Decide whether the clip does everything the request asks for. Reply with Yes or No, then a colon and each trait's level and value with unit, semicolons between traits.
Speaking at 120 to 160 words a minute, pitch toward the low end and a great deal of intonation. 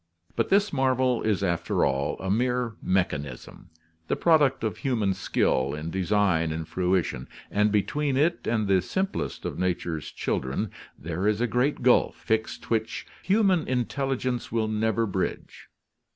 Yes: average, 145 wpm; low, 110 Hz; wide, 5.9 semitones